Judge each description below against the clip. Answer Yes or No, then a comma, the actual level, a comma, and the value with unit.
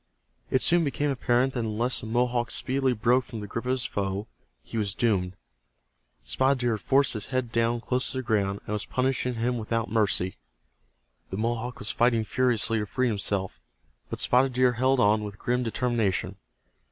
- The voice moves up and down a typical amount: Yes, average, 3.0 semitones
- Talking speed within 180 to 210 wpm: Yes, average, 185 wpm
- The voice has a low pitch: Yes, low, 120 Hz